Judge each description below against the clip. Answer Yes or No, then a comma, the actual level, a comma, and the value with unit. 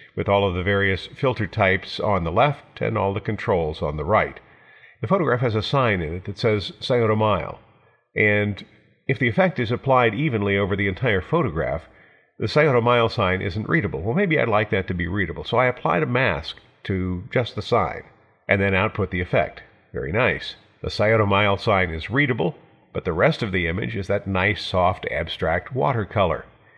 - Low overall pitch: Yes, low, 105 Hz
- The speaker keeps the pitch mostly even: No, average, 3.8 semitones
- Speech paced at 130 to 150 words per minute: No, average, 195 wpm